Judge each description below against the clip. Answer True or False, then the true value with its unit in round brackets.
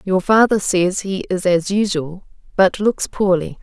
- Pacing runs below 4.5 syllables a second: True (4.1 syllables/s)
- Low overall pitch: False (190 Hz)